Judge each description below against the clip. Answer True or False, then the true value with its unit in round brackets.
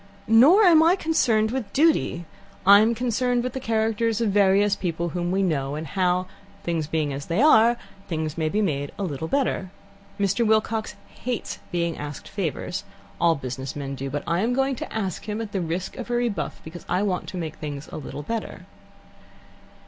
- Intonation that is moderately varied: False (6.1 semitones)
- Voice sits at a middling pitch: False (195 Hz)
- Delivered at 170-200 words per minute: True (190 wpm)